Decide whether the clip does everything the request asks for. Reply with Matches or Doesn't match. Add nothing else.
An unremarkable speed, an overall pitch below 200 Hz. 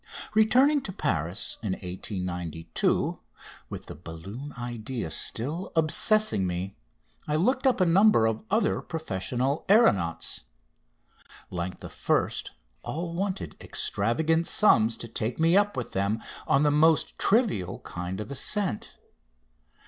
Doesn't match